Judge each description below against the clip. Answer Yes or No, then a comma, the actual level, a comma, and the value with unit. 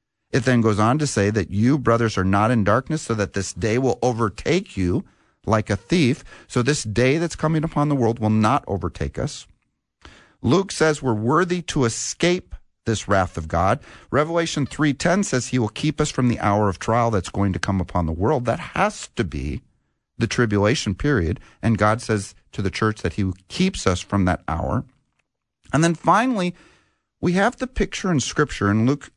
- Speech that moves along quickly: No, average, 195 wpm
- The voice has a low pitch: Yes, low, 115 Hz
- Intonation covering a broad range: Yes, wide, 6.6 semitones